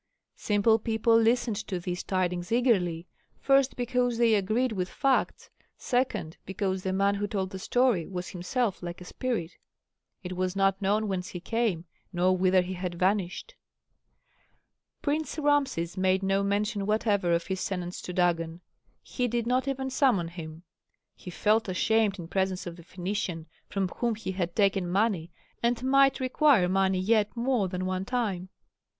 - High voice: Yes, high, 195 Hz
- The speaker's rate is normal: Yes, average, 160 wpm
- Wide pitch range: No, average, 4.4 semitones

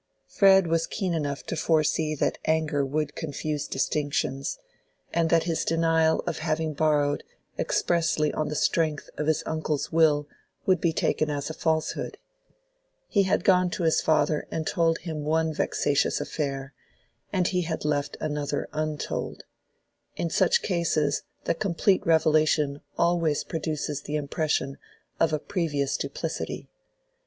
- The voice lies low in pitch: No, medium, 155 Hz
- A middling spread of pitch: No, narrow, 1.9 semitones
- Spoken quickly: No, average, 140 wpm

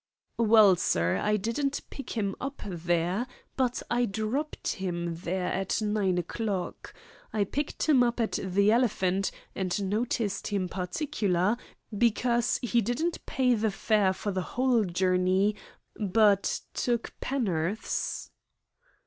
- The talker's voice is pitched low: No, high, 210 Hz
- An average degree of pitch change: Yes, average, 4.2 semitones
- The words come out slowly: Yes, slow, 125 wpm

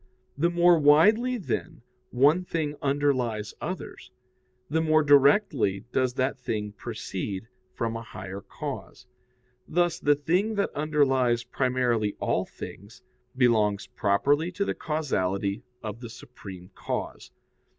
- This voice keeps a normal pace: No, slow, 120 wpm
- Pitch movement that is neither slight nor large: No, wide, 6.0 semitones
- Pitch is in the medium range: No, low, 130 Hz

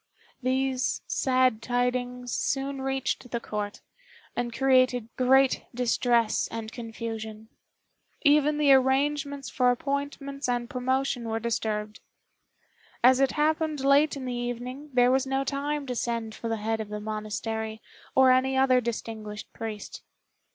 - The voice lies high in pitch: Yes, very high, 250 Hz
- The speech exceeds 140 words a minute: No, slow, 135 wpm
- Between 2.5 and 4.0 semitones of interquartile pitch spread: Yes, average, 2.9 semitones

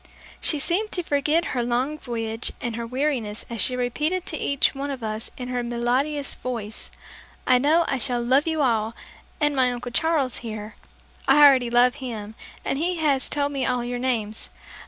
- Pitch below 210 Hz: No, very high, 255 Hz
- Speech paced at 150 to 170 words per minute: No, average, 185 wpm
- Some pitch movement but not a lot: Yes, average, 3.5 semitones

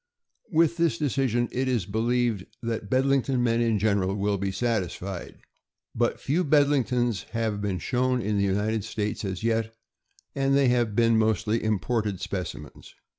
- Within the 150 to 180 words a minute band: Yes, average, 160 wpm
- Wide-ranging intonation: No, average, 3.5 semitones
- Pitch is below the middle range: Yes, low, 115 Hz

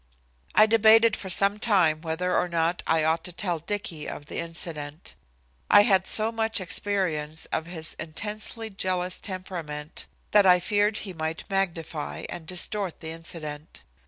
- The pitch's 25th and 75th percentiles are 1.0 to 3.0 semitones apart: No, average, 4.2 semitones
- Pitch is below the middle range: No, medium, 180 Hz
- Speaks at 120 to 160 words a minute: Yes, average, 155 wpm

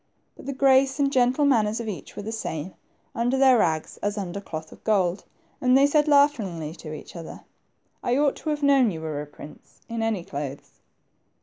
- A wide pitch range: Yes, wide, 8.0 semitones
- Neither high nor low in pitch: No, high, 225 Hz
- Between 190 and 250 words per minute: Yes, average, 200 wpm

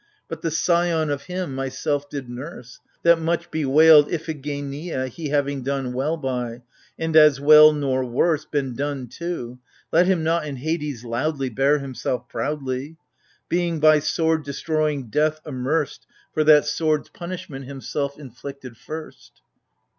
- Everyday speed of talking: Yes, average, 145 wpm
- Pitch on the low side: No, medium, 145 Hz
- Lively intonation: No, average, 2.9 semitones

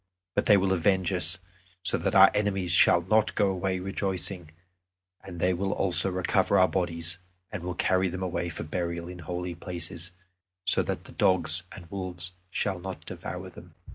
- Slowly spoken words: No, average, 175 wpm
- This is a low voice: Yes, very low, 90 Hz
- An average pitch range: No, narrow, 1.6 semitones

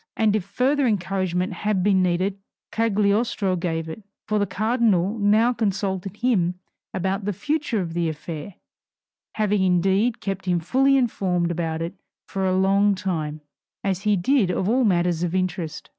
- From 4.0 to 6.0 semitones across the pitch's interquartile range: No, average, 3.2 semitones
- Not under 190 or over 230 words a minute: No, average, 160 wpm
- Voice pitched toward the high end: Yes, high, 195 Hz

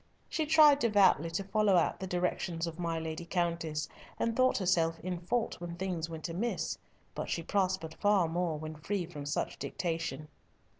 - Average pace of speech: Yes, average, 170 wpm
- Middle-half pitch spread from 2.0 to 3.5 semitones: Yes, average, 3.0 semitones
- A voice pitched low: No, medium, 175 Hz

